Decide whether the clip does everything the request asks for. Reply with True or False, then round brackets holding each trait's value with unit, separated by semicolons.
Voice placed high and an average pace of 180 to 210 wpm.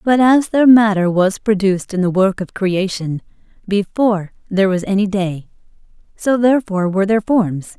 False (200 Hz; 160 wpm)